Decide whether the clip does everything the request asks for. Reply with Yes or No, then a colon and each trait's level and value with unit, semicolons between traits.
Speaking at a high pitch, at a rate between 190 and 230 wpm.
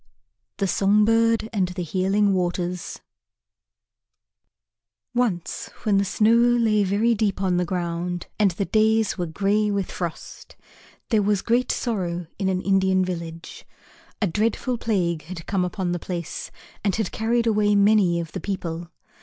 No: high, 195 Hz; average, 150 wpm